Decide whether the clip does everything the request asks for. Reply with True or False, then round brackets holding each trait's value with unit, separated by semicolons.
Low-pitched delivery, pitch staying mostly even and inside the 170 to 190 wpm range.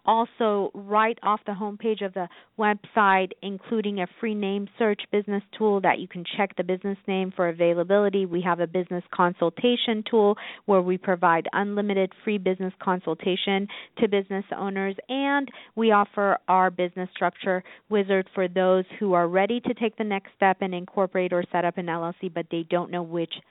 False (195 Hz; 2.3 semitones; 175 wpm)